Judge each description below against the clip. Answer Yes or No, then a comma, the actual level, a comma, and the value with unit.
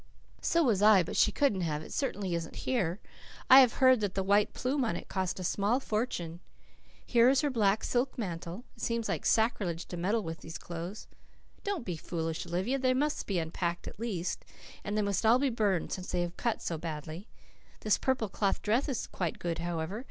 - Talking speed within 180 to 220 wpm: Yes, fast, 205 wpm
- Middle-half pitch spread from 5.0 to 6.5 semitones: Yes, wide, 5.5 semitones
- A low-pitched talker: No, high, 200 Hz